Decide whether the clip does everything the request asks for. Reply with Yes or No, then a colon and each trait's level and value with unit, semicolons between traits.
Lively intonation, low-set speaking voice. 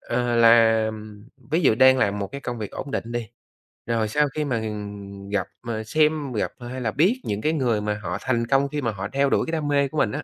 No: average, 4.3 semitones; low, 120 Hz